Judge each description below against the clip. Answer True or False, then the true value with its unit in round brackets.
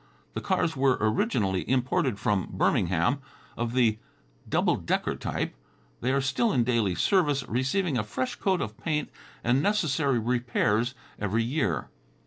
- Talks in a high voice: False (125 Hz)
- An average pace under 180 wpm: True (140 wpm)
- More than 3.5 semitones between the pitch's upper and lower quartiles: True (4.6 semitones)